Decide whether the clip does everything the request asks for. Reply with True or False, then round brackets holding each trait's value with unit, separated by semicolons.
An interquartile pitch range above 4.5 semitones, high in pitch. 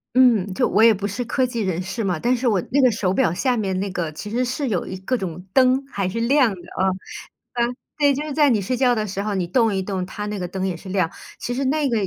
True (5.0 semitones; 215 Hz)